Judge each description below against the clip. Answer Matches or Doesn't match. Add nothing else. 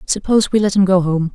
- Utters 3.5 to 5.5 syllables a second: Doesn't match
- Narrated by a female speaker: Matches